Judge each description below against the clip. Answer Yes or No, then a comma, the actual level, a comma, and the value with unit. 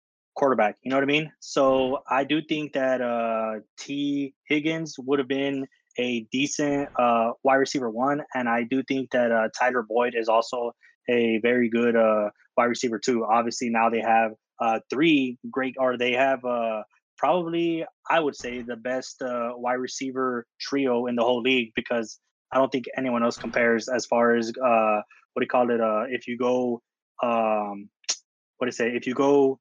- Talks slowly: No, average, 185 wpm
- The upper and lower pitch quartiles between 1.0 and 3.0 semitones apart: Yes, narrow, 2.5 semitones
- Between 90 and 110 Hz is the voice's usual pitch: No, low, 125 Hz